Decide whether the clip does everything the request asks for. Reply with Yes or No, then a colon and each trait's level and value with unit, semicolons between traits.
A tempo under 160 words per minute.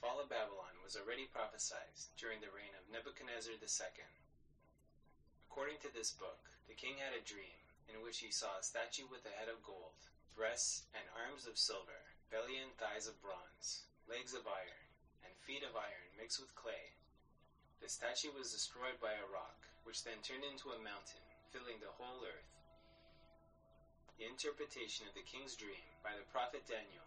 No: average, 175 wpm